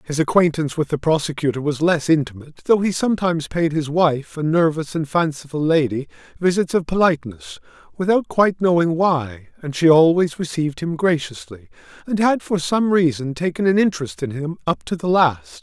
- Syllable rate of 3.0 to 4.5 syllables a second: No, 5.5 syllables/s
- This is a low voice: No, medium, 160 Hz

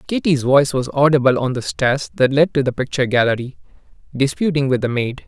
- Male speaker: Yes, male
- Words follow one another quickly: No, average, 195 wpm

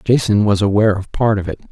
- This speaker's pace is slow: No, fast, 245 wpm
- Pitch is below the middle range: Yes, low, 105 Hz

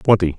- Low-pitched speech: Yes, very low, 95 Hz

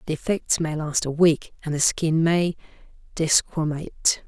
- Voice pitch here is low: No, medium, 160 Hz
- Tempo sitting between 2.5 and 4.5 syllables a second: No, 4.9 syllables/s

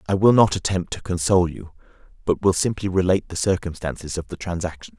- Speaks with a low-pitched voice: Yes, very low, 90 Hz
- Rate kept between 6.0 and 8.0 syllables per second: Yes, 6.2 syllables/s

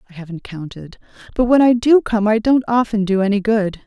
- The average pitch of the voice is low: No, high, 215 Hz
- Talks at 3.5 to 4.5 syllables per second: No, 5.6 syllables/s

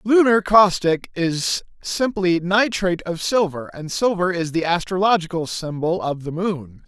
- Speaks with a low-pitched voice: No, medium, 180 Hz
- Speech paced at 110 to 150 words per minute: Yes, average, 140 wpm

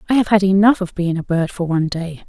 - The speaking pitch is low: No, medium, 185 Hz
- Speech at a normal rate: No, fast, 290 wpm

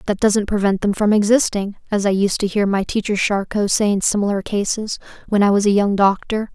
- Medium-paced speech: No, fast, 220 wpm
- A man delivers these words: No, female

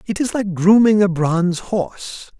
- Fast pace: No, average, 175 wpm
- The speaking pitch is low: No, high, 195 Hz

